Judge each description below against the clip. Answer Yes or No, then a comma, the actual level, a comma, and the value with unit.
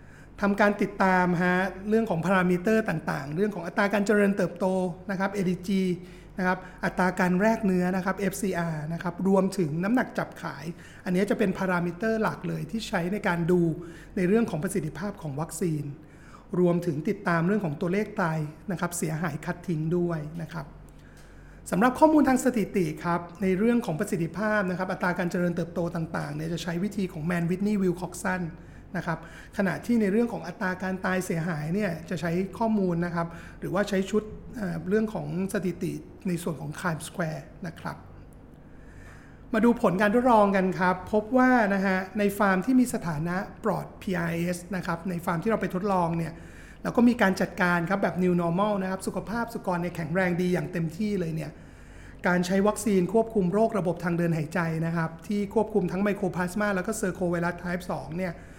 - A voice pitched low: No, medium, 185 Hz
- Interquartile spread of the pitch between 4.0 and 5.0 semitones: No, average, 2.9 semitones